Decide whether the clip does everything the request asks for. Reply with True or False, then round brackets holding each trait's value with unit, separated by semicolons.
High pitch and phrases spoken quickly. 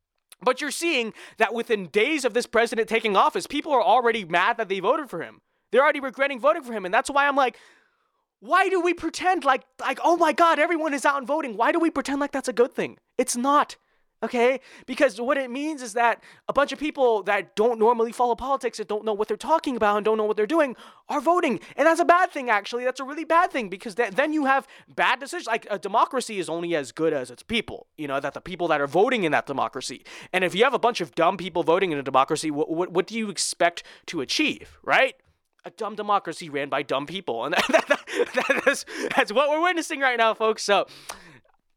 True (245 Hz; 245 wpm)